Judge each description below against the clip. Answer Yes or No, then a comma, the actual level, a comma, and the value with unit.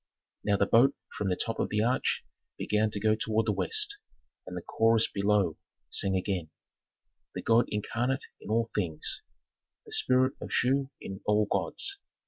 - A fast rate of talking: No, average, 165 wpm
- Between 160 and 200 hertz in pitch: No, low, 110 Hz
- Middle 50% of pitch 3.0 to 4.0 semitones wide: Yes, average, 3.6 semitones